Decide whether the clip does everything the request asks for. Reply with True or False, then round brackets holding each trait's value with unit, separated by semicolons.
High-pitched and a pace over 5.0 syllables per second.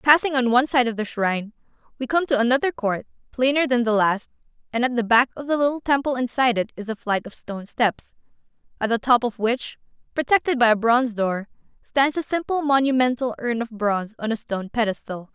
True (240 Hz; 5.9 syllables/s)